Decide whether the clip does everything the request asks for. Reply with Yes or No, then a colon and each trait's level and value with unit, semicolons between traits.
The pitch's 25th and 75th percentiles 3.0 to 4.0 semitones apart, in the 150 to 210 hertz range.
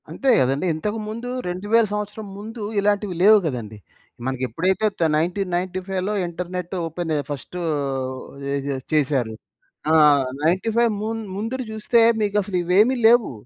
No: average, 5.2 semitones; medium, 185 Hz